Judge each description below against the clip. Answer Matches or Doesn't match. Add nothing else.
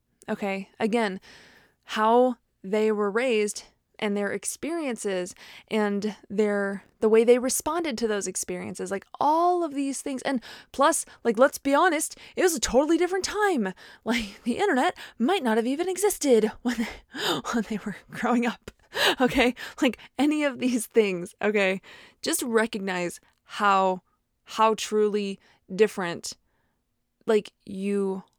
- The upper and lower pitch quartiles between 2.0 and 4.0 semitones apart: Doesn't match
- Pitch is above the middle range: Matches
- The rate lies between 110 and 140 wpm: Matches